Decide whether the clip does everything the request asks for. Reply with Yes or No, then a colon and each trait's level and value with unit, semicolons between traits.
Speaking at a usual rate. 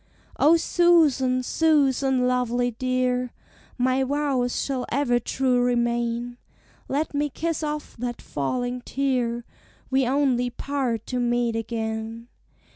No: slow, 115 wpm